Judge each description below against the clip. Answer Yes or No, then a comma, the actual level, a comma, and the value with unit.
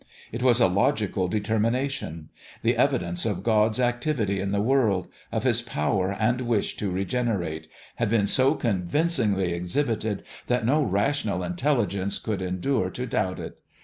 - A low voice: Yes, low, 105 Hz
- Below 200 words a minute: Yes, average, 150 wpm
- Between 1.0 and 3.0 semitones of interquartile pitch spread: No, average, 4.7 semitones